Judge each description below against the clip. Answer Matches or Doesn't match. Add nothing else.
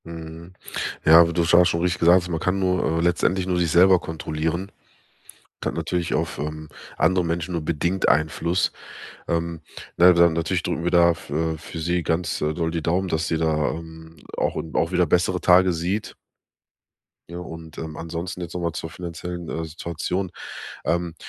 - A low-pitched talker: Matches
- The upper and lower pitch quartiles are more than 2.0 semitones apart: Doesn't match